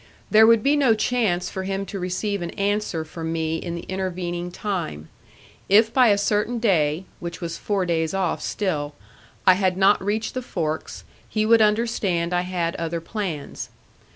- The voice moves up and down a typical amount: Yes, average, 3.8 semitones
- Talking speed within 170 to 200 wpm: Yes, average, 175 wpm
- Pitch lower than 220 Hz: Yes, high, 190 Hz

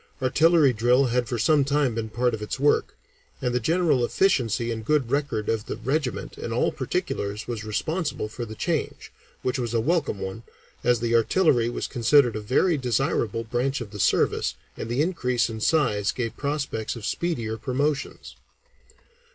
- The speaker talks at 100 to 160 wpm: No, average, 175 wpm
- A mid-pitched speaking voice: No, low, 120 Hz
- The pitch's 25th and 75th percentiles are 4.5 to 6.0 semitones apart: No, average, 4.1 semitones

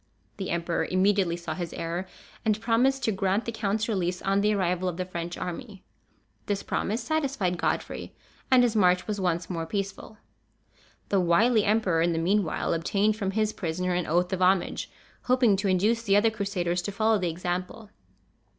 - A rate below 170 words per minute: No, average, 180 wpm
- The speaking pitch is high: Yes, high, 195 Hz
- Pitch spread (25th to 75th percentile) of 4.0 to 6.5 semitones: No, average, 3.4 semitones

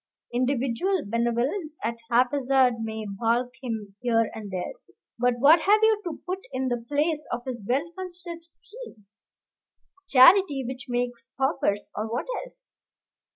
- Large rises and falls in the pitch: Yes, wide, 5.8 semitones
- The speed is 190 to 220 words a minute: No, average, 140 wpm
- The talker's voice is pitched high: Yes, very high, 255 Hz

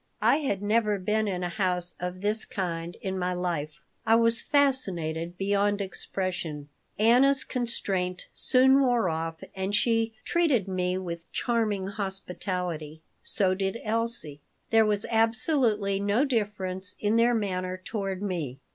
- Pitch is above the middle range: Yes, high, 200 Hz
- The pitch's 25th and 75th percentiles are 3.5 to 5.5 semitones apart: Yes, average, 3.8 semitones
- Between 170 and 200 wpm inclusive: No, average, 140 wpm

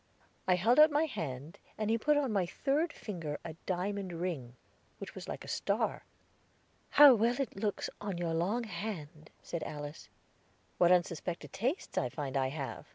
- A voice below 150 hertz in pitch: No, medium, 185 Hz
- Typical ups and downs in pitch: No, wide, 6.3 semitones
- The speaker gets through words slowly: No, average, 170 wpm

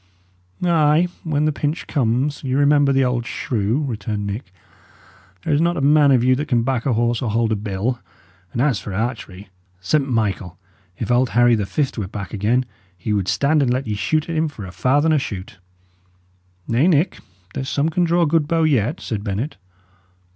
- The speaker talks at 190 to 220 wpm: Yes, average, 195 wpm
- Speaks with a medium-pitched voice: No, low, 125 Hz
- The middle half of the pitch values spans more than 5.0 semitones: Yes, wide, 5.5 semitones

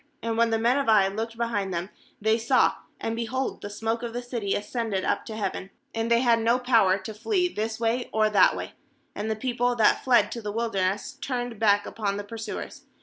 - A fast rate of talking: Yes, fast, 215 wpm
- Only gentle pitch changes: Yes, narrow, 2.3 semitones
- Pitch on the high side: Yes, high, 225 Hz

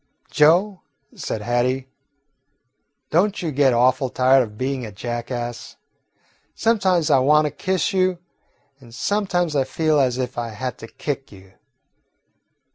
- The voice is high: No, low, 135 Hz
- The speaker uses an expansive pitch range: Yes, wide, 5.7 semitones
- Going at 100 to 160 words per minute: Yes, slow, 135 wpm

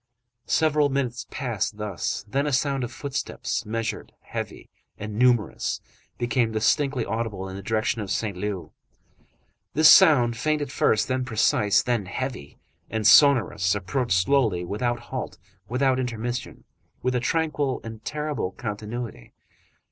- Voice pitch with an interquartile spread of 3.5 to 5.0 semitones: Yes, average, 4.1 semitones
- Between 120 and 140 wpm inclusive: Yes, slow, 135 wpm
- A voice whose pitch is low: Yes, low, 120 Hz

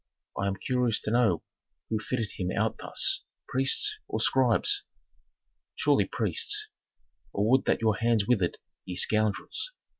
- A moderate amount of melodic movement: Yes, average, 4.1 semitones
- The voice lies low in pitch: Yes, low, 115 Hz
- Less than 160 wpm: Yes, average, 140 wpm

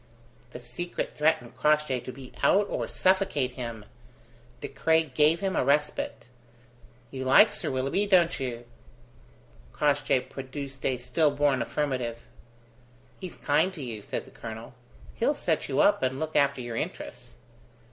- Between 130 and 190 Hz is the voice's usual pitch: Yes, low, 135 Hz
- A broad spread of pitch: No, average, 3.3 semitones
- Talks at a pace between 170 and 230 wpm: No, average, 145 wpm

